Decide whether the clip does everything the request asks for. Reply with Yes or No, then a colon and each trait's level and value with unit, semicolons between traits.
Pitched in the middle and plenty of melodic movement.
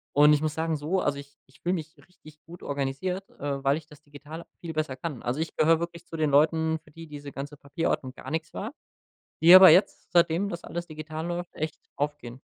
No: medium, 155 Hz; narrow, 2.6 semitones